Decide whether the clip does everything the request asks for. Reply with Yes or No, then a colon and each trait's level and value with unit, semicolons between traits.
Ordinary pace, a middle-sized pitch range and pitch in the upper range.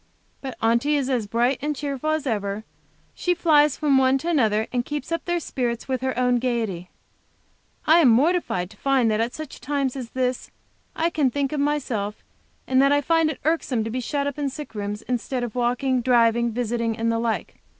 No: fast, 210 wpm; average, 3.9 semitones; very high, 255 Hz